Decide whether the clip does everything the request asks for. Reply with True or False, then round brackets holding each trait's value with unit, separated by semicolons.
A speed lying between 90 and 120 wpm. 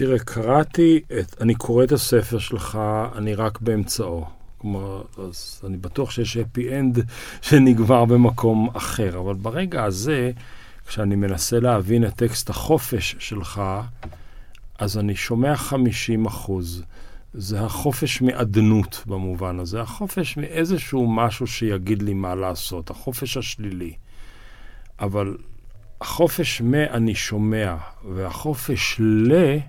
True (115 wpm)